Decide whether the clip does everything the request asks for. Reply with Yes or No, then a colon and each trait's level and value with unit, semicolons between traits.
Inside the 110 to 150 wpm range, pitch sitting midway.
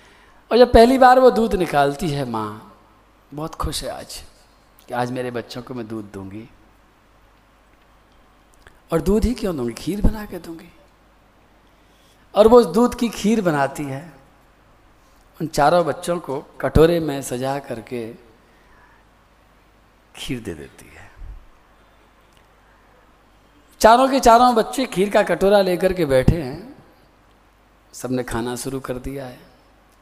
Yes: average, 135 wpm; medium, 145 Hz